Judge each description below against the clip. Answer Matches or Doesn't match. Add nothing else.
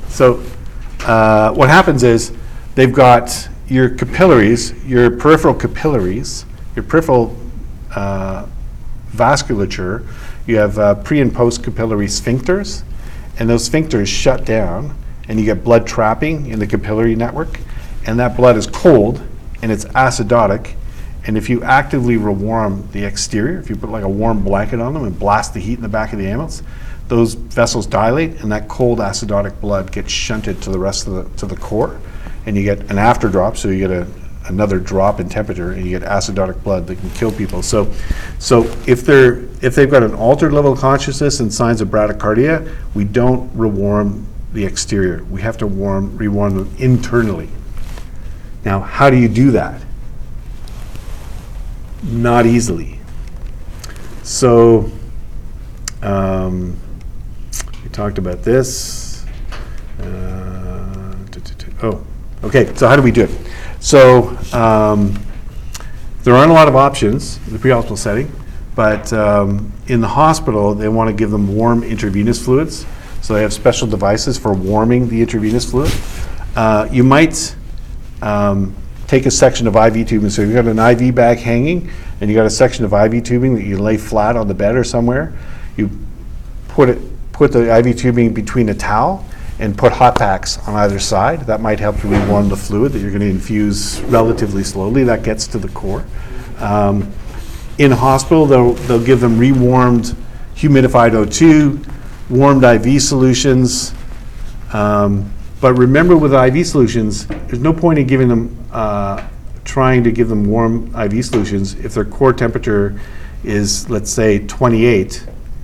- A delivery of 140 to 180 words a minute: Matches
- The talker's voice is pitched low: Matches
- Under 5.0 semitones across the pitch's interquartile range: Matches